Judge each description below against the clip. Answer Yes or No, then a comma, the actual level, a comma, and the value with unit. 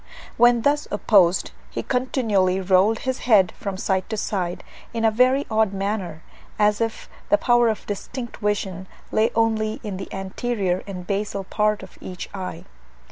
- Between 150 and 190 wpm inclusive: Yes, average, 160 wpm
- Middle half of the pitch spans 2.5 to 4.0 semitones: Yes, average, 3.0 semitones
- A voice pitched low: No, high, 210 Hz